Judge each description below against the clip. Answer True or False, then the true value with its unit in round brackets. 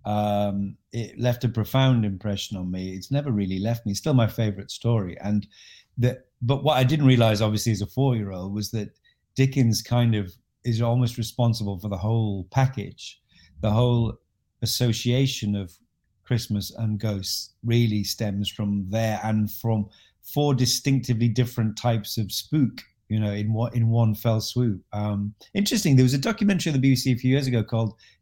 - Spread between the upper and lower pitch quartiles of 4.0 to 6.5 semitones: False (3.1 semitones)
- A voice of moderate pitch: False (115 Hz)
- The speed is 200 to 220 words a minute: False (180 wpm)